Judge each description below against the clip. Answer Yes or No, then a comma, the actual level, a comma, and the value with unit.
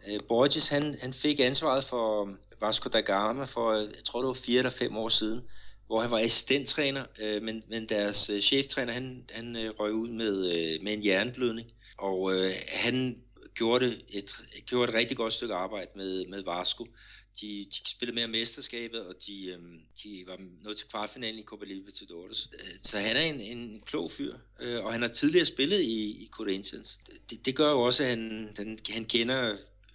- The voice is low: Yes, low, 115 Hz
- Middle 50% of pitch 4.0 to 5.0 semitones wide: No, average, 2.9 semitones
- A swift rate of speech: No, average, 175 wpm